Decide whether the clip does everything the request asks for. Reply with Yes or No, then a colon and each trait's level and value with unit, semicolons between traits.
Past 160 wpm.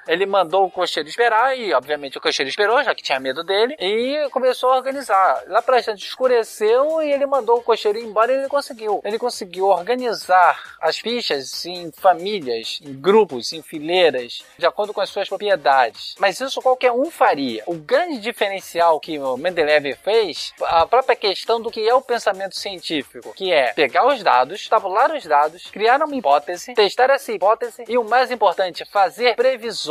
Yes: average, 180 wpm